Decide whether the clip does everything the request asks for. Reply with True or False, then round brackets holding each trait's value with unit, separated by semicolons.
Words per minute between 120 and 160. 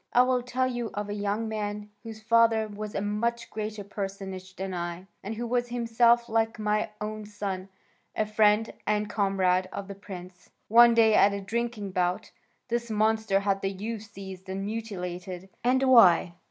False (175 wpm)